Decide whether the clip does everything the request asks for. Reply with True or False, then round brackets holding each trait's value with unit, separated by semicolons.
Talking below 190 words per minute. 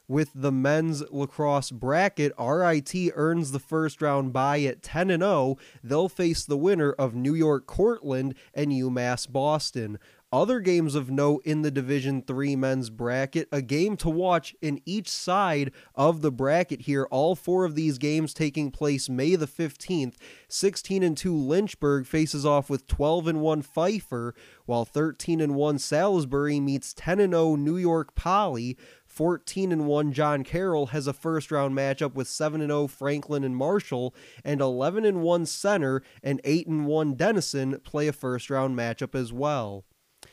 True (160 wpm)